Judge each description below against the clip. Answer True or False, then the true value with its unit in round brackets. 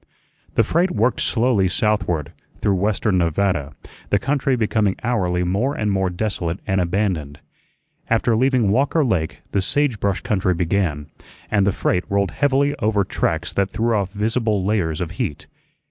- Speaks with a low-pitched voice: True (100 Hz)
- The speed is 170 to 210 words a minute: False (155 wpm)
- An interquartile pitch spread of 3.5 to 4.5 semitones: True (4.0 semitones)